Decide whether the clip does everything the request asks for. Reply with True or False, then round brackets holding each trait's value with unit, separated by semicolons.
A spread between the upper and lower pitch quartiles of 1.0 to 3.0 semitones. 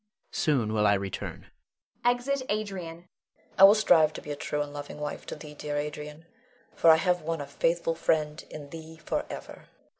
True (2.6 semitones)